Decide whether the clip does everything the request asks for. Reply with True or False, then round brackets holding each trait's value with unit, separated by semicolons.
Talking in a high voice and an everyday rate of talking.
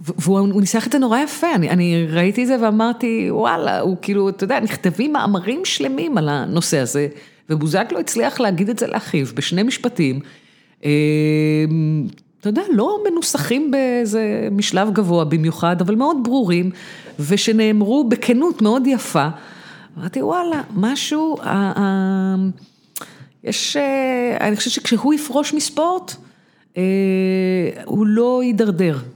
True (210 Hz; 130 wpm)